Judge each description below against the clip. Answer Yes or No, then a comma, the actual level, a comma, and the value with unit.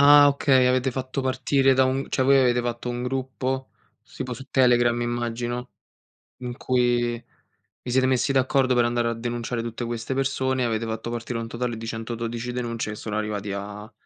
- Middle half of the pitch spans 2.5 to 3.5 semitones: No, narrow, 1.9 semitones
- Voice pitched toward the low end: Yes, low, 120 Hz